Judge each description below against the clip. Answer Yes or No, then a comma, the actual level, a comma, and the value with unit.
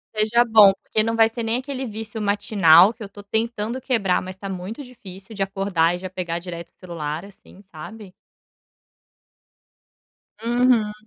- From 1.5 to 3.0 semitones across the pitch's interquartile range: No, average, 3.4 semitones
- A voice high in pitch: Yes, high, 205 Hz